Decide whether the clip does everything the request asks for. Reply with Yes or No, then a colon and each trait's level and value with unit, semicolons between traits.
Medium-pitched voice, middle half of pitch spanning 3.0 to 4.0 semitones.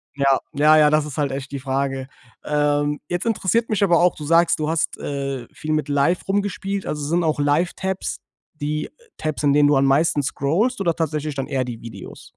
Yes: medium, 150 Hz; average, 3.4 semitones